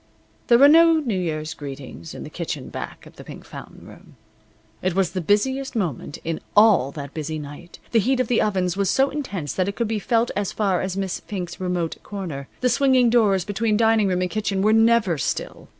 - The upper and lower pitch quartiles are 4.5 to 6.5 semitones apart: Yes, average, 4.9 semitones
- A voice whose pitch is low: No, high, 195 Hz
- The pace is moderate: No, fast, 215 wpm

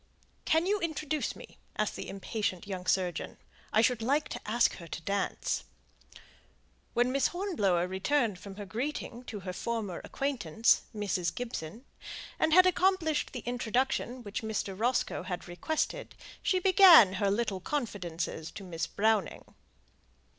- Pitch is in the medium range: No, high, 225 Hz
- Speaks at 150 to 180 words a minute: No, average, 140 wpm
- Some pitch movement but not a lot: No, wide, 6.9 semitones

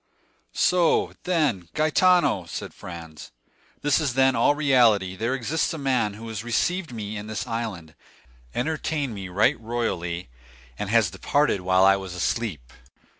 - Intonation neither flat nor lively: No, wide, 6.9 semitones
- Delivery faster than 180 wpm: No, average, 145 wpm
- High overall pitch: No, low, 115 Hz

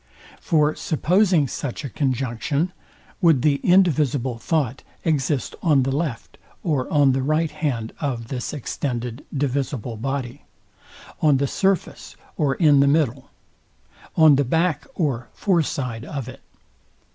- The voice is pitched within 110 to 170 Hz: Yes, medium, 140 Hz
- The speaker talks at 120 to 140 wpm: Yes, slow, 135 wpm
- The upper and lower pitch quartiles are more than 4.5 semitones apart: No, average, 3.4 semitones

